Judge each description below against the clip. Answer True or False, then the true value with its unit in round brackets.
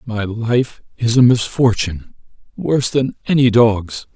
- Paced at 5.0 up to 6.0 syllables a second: False (4.2 syllables/s)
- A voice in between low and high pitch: False (115 Hz)